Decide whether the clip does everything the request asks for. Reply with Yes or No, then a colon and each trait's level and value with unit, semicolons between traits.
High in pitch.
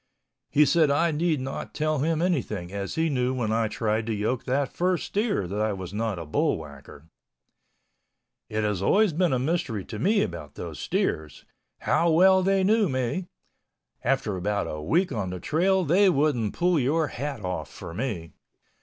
No: low, 130 Hz